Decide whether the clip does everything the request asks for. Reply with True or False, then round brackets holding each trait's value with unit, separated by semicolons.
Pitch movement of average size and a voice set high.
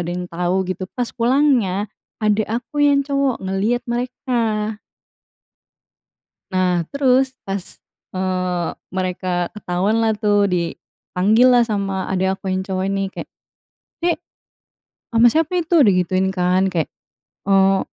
True (4.6 semitones; 195 Hz)